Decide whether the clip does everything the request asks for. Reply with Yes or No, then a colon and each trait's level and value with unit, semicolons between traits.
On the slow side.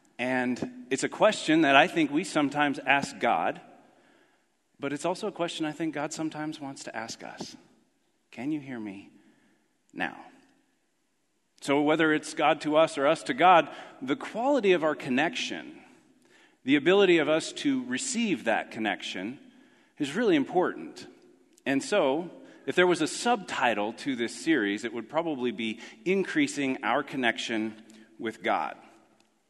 No: average, 150 wpm